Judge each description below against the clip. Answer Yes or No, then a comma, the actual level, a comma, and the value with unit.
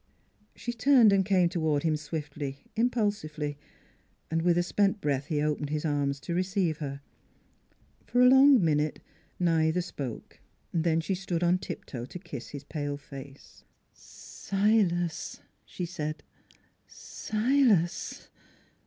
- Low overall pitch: No, medium, 165 Hz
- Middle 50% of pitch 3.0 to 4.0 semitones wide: No, average, 4.8 semitones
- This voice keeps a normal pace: No, slow, 130 wpm